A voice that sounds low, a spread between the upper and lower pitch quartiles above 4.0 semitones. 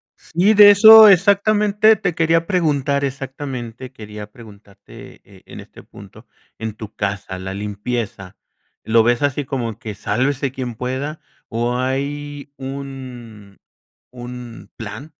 Yes: low, 130 Hz; average, 4.7 semitones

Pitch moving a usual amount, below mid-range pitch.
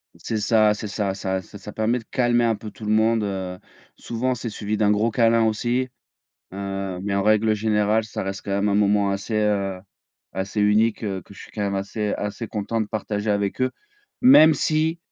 No: narrow, 2.1 semitones; low, 105 Hz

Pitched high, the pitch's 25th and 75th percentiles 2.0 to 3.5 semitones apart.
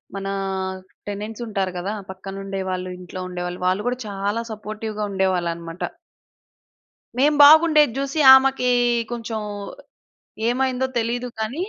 No: high, 215 Hz; average, 4.9 semitones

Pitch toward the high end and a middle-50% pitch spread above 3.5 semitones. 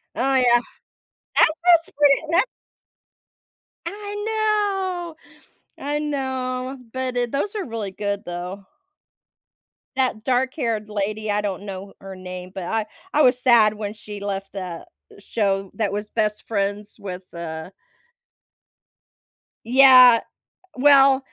Yes: high, 230 Hz; average, 5.3 semitones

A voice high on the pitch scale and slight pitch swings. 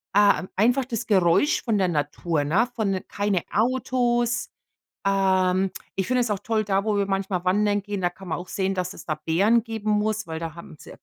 No: high, 200 Hz; average, 3.1 semitones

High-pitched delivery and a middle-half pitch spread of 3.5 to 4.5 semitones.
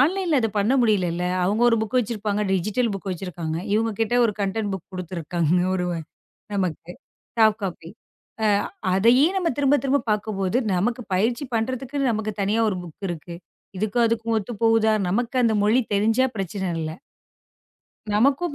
Yes: high, 215 Hz; average, 3.9 semitones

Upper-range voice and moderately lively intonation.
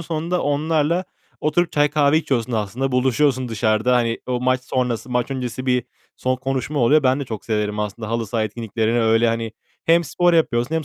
No: low, 125 Hz; average, 4.3 semitones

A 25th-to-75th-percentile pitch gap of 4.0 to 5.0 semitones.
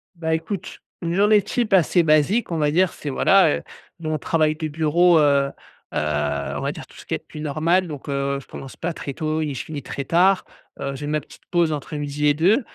No: average, 3.1 semitones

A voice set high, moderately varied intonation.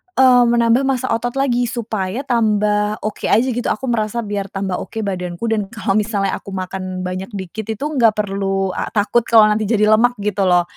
Yes: high, 215 Hz; average, 3.3 semitones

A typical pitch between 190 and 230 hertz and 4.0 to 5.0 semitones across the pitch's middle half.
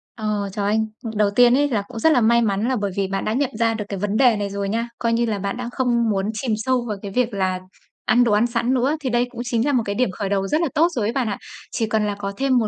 No: high, 225 Hz; average, 3.3 semitones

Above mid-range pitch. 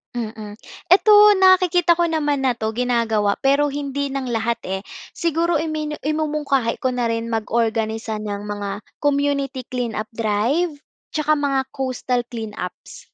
Yes: very high, 255 Hz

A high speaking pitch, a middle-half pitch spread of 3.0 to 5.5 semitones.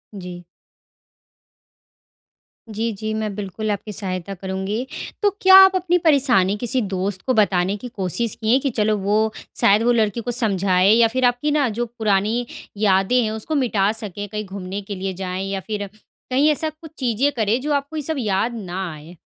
Yes: high, 215 Hz; average, 4.1 semitones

